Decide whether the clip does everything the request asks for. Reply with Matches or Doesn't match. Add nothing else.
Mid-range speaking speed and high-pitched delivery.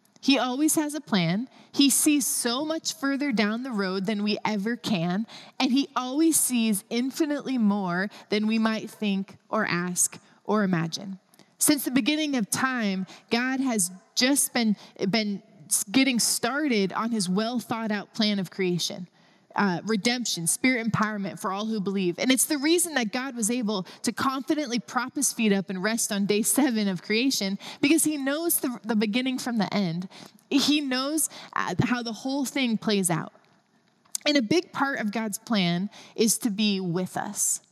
Matches